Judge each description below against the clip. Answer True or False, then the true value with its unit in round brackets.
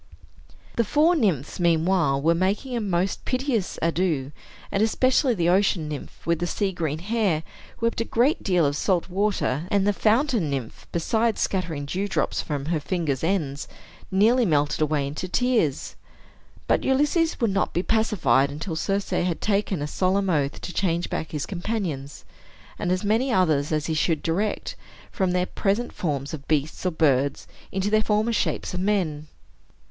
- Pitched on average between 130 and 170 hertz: False (180 Hz)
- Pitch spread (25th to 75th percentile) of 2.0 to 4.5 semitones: False (5.4 semitones)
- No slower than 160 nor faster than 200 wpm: True (165 wpm)